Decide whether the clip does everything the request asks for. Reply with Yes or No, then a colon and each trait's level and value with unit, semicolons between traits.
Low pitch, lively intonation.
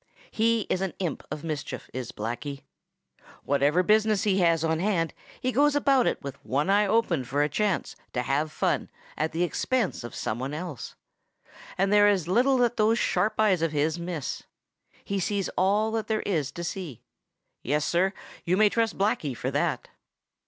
No: medium, 180 Hz; wide, 5.9 semitones